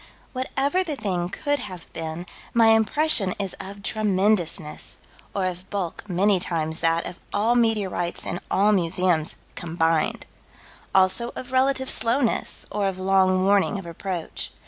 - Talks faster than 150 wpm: No, average, 140 wpm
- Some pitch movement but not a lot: Yes, average, 4.2 semitones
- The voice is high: Yes, high, 195 Hz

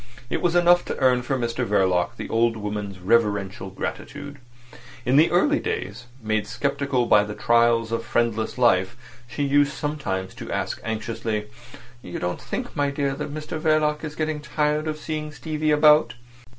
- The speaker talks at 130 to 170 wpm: Yes, average, 165 wpm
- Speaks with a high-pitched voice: No, low, 125 Hz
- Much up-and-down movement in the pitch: Yes, wide, 5.7 semitones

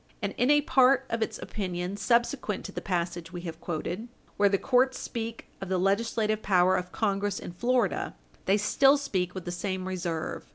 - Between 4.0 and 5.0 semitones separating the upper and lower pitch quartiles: Yes, average, 4.6 semitones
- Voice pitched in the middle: No, high, 200 Hz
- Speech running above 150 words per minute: Yes, average, 190 wpm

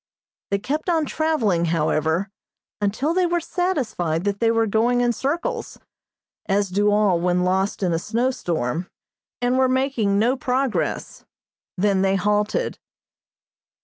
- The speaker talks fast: No, average, 140 wpm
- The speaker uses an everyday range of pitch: No, wide, 5.7 semitones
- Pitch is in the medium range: No, high, 210 Hz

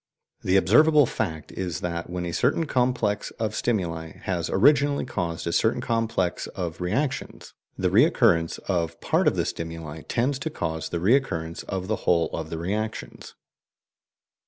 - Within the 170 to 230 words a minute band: No, average, 155 wpm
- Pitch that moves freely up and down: Yes, wide, 6.2 semitones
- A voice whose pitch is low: Yes, very low, 90 Hz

